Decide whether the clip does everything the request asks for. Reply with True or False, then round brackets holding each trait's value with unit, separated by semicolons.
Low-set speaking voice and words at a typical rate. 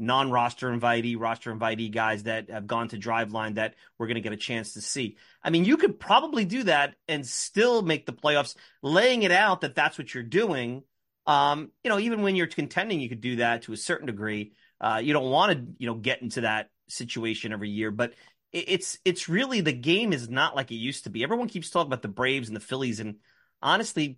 False (125 Hz; 230 wpm)